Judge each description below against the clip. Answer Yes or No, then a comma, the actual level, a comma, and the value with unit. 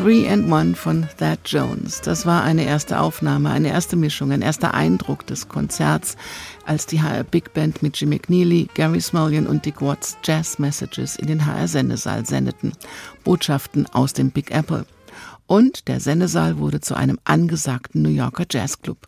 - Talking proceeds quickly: No, average, 170 wpm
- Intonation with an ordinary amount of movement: Yes, average, 3.7 semitones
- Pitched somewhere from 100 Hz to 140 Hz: No, medium, 150 Hz